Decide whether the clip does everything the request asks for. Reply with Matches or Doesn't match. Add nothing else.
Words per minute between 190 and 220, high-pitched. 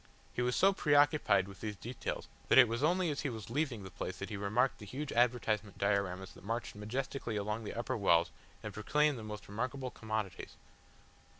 Doesn't match